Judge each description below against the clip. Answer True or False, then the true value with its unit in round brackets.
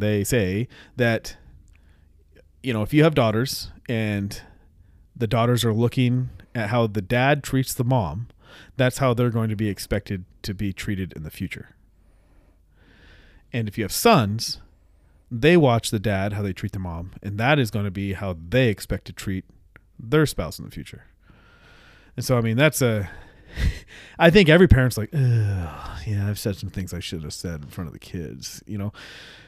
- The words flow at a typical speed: True (185 wpm)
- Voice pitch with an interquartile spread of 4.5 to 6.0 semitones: True (4.8 semitones)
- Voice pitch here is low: True (105 Hz)